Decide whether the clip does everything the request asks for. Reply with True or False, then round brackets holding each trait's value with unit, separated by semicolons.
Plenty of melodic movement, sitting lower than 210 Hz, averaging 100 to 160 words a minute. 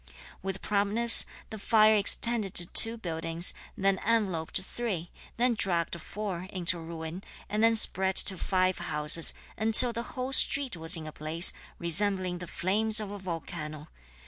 False (4.4 semitones; 190 Hz; 150 wpm)